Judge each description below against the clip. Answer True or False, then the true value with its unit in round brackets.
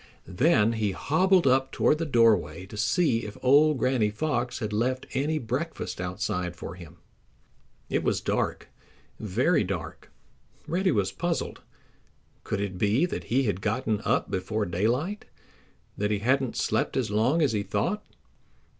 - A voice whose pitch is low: True (115 Hz)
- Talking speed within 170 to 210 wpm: False (145 wpm)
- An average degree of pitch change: False (5.8 semitones)